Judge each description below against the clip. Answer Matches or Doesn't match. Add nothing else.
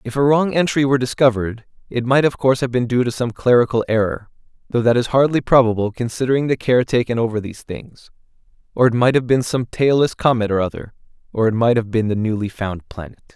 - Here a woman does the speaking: Doesn't match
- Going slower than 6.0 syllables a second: Doesn't match